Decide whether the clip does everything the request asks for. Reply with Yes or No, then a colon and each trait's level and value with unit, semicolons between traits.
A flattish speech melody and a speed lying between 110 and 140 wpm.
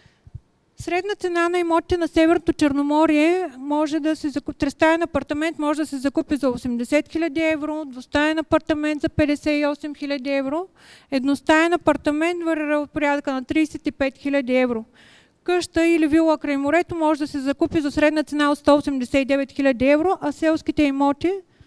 No: narrow, 2.2 semitones; average, 150 wpm